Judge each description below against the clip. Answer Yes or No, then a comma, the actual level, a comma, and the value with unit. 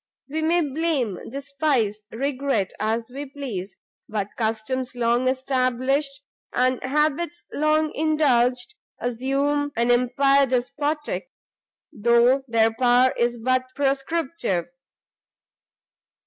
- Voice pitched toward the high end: Yes, very high, 260 Hz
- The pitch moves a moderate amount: Yes, average, 3.2 semitones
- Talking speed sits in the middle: No, slow, 95 wpm